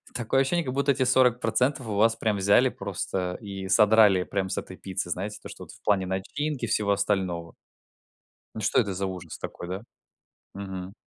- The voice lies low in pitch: Yes, low, 100 Hz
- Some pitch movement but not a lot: Yes, average, 3.6 semitones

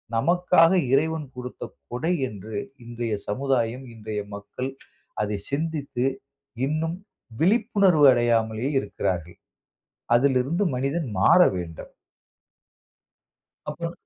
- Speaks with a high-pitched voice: No, low, 130 Hz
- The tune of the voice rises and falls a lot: Yes, wide, 6.3 semitones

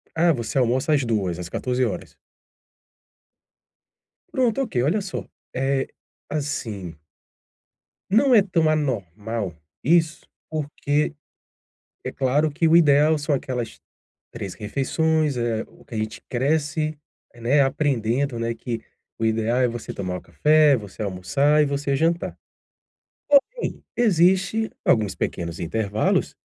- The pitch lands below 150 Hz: Yes, low, 135 Hz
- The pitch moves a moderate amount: No, wide, 5.7 semitones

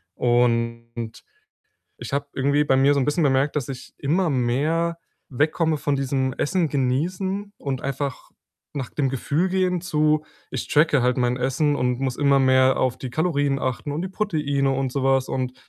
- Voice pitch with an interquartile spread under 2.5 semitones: No, average, 2.8 semitones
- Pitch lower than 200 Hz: Yes, medium, 140 Hz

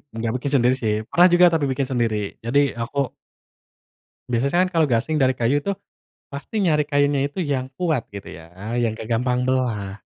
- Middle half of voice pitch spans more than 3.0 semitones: Yes, average, 3.9 semitones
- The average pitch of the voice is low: Yes, low, 130 Hz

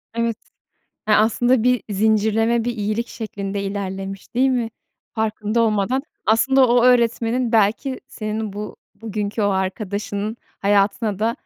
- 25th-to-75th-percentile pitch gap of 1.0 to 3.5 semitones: Yes, narrow, 2.5 semitones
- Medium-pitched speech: No, high, 220 Hz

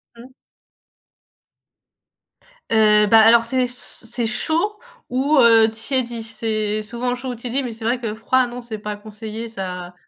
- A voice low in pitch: No, high, 230 Hz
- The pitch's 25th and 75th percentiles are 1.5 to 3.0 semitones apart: Yes, narrow, 2.4 semitones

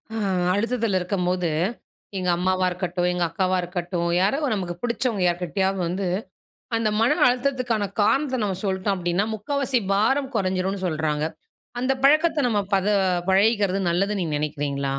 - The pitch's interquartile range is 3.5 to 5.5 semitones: Yes, average, 4.2 semitones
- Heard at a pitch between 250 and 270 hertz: No, high, 195 Hz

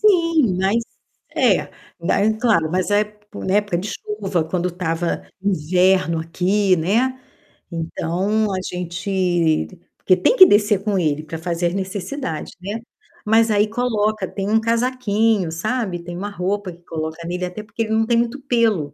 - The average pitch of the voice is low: No, high, 195 Hz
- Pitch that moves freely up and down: No, average, 3.9 semitones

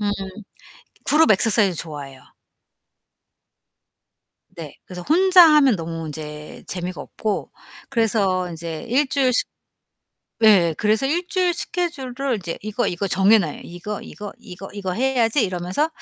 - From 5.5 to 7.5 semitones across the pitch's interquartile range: Yes, wide, 7.1 semitones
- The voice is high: Yes, high, 205 Hz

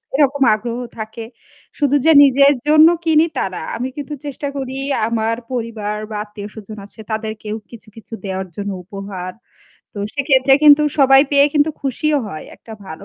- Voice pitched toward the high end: Yes, high, 240 Hz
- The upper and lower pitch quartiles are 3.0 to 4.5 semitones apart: No, average, 5.0 semitones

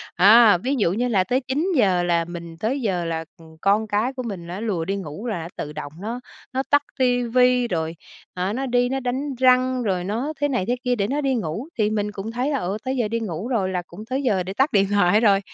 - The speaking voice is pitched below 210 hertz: No, high, 215 Hz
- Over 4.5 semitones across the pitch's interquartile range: Yes, wide, 5.4 semitones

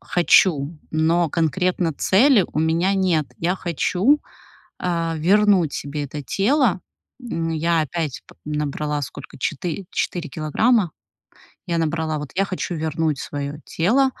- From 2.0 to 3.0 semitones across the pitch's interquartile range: No, average, 3.6 semitones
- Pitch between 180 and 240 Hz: No, medium, 165 Hz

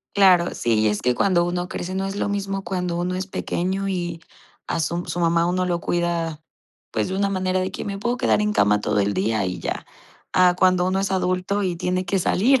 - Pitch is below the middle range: No, medium, 180 Hz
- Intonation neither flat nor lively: No, narrow, 2.1 semitones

